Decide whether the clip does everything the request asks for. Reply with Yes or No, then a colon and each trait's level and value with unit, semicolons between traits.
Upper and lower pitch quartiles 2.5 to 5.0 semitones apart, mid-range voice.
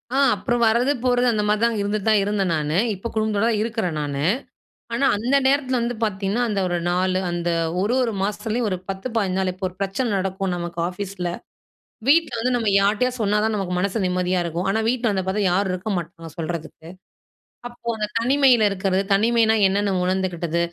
No: average, 4.0 semitones; high, 200 Hz